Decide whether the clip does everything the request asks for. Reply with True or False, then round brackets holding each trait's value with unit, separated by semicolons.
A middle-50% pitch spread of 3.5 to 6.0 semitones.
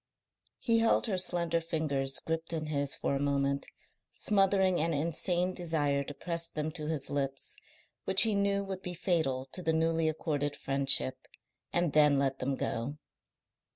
True (3.9 semitones)